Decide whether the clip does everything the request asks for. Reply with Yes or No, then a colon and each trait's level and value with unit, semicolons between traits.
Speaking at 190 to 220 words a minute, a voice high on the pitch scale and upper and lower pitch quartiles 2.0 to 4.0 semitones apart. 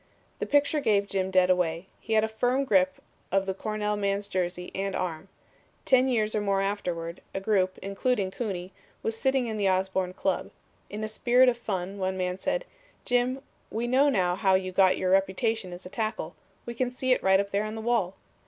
Yes: fast, 205 wpm; high, 200 Hz; average, 3.3 semitones